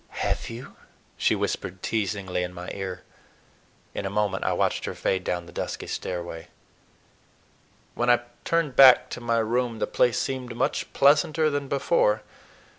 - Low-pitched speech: Yes, low, 115 Hz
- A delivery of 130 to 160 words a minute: Yes, average, 155 wpm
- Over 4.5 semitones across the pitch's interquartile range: Yes, wide, 5.5 semitones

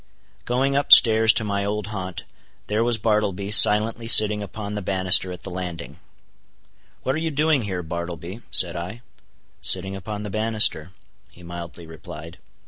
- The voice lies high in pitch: No, low, 100 Hz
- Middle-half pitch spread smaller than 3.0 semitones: No, average, 3.6 semitones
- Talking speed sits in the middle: Yes, average, 155 wpm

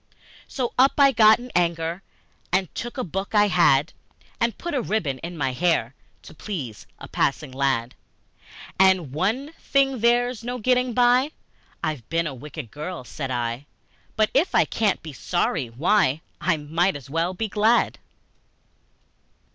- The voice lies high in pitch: No, medium, 180 Hz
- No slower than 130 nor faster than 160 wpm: Yes, average, 155 wpm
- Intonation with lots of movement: Yes, wide, 8.1 semitones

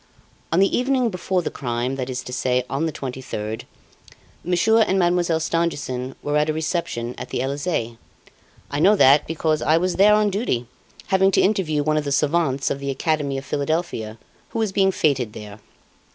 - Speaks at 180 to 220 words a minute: Yes, average, 185 wpm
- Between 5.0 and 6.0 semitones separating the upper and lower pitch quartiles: Yes, wide, 5.4 semitones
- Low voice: No, medium, 155 Hz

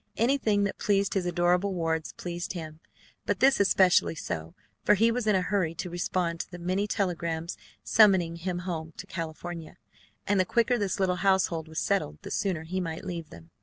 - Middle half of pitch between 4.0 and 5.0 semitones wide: No, average, 3.1 semitones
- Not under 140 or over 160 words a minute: No, average, 190 wpm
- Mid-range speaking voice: Yes, medium, 180 Hz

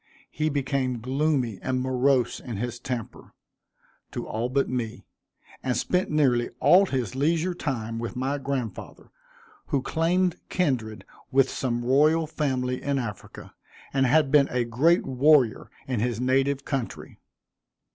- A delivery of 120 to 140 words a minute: Yes, slow, 135 wpm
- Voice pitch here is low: Yes, low, 130 Hz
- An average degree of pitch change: Yes, average, 3.0 semitones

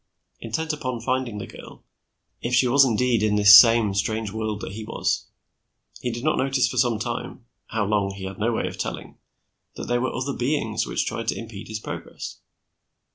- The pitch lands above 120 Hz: No, low, 115 Hz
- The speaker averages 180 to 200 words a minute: Yes, average, 195 wpm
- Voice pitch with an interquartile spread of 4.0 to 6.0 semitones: No, average, 3.1 semitones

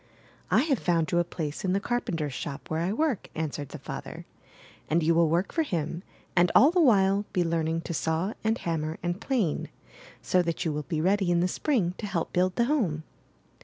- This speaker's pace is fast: Yes, fast, 210 wpm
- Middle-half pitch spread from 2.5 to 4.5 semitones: Yes, average, 4.1 semitones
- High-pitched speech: No, medium, 175 Hz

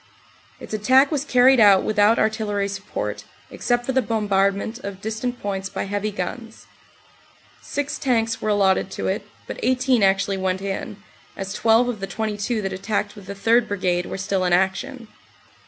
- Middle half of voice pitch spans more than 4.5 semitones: No, average, 3.2 semitones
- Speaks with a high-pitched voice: Yes, high, 210 Hz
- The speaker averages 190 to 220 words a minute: No, average, 170 wpm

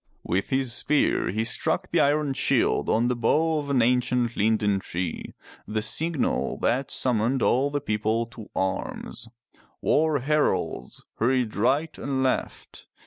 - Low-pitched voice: Yes, low, 125 Hz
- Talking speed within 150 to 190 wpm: No, average, 140 wpm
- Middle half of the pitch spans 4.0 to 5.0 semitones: Yes, average, 4.3 semitones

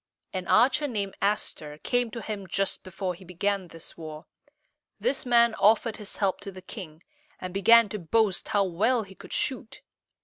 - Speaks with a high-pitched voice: Yes, high, 200 Hz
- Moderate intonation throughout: Yes, average, 3.8 semitones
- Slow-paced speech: No, average, 175 wpm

